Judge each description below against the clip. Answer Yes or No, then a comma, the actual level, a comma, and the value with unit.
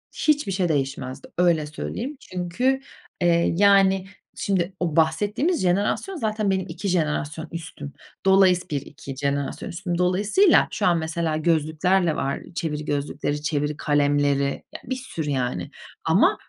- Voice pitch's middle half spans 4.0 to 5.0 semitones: Yes, average, 4.6 semitones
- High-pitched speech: No, medium, 170 Hz